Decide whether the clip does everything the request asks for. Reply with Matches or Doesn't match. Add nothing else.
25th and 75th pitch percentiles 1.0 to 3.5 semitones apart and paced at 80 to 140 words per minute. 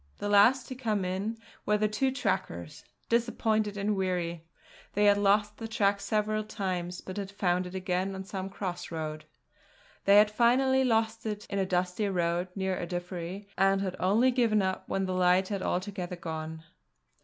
Doesn't match